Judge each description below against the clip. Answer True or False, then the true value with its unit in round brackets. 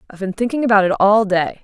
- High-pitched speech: True (205 Hz)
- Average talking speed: False (255 wpm)